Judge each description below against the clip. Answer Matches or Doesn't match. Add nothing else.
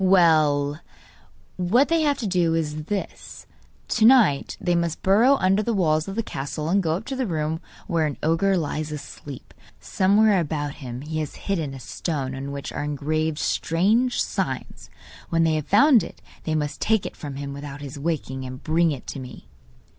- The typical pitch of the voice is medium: Matches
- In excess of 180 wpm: Matches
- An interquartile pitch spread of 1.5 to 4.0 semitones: Doesn't match